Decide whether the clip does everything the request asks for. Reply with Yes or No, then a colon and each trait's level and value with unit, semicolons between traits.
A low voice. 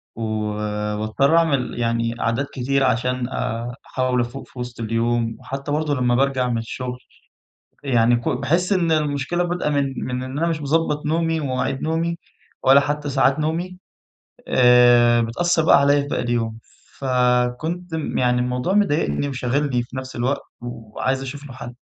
Yes: low, 130 Hz